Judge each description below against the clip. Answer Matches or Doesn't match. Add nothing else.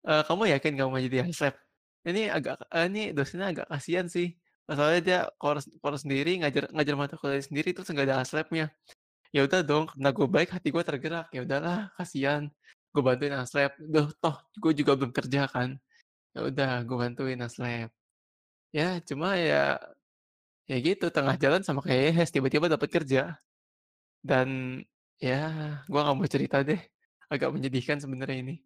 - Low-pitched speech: Doesn't match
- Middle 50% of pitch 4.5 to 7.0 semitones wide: Doesn't match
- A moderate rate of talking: Doesn't match